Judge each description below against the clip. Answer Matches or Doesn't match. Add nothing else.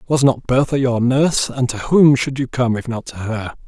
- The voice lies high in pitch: Doesn't match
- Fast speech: Matches